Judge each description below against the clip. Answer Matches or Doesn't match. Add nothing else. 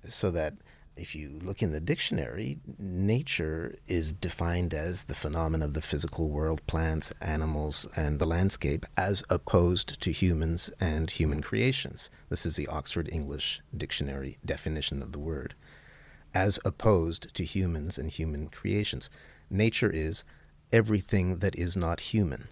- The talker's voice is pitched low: Matches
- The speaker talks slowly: Doesn't match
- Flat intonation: Doesn't match